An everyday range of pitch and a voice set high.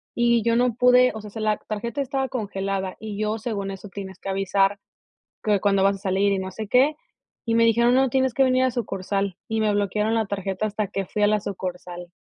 Yes: average, 3.1 semitones; high, 210 Hz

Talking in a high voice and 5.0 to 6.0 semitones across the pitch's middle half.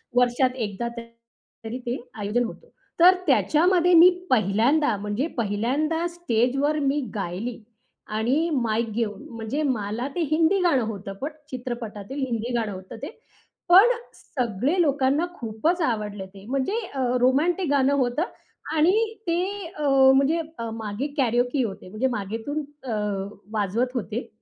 Yes: very high, 250 Hz; wide, 5.4 semitones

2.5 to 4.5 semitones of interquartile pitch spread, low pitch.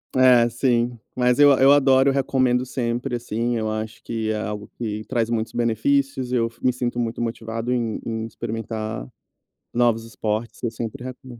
No: narrow, 2.0 semitones; low, 120 Hz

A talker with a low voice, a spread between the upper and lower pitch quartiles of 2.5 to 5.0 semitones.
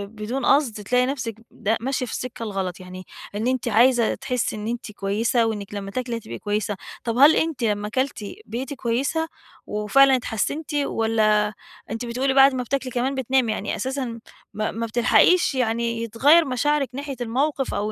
No: high, 240 Hz; average, 3.7 semitones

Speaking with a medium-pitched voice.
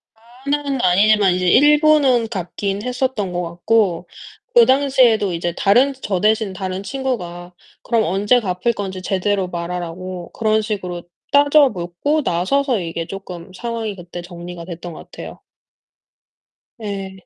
No: high, 195 Hz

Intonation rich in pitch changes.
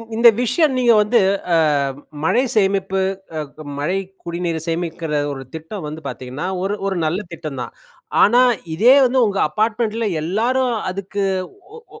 Yes: wide, 6.0 semitones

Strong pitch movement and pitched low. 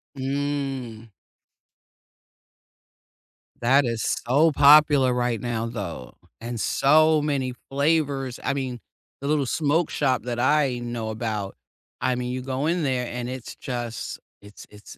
No: average, 3.1 semitones; low, 130 Hz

